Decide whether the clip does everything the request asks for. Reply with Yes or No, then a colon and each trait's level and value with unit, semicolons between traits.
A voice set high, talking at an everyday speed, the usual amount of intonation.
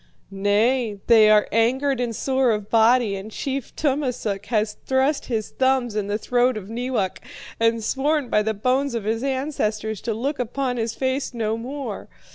Yes: high, 235 Hz; average, 170 wpm; average, 3.6 semitones